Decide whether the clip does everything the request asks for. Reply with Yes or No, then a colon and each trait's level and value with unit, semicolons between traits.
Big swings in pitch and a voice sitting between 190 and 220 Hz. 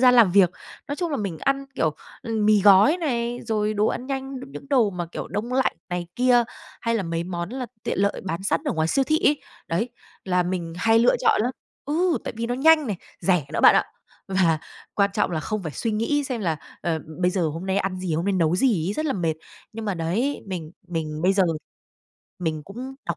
Yes: wide, 6.1 semitones; high, 200 Hz